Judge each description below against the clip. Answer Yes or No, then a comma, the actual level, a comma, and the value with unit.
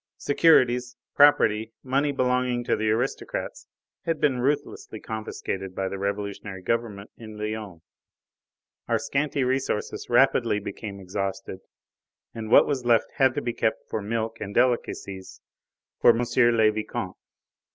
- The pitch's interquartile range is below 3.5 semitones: No, average, 3.9 semitones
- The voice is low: Yes, low, 115 Hz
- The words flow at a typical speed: No, slow, 130 wpm